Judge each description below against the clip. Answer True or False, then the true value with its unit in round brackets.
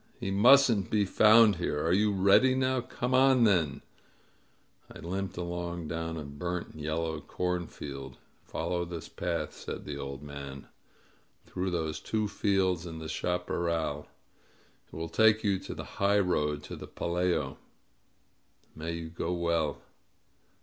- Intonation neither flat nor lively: True (4.1 semitones)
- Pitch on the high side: False (85 Hz)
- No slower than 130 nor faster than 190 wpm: True (150 wpm)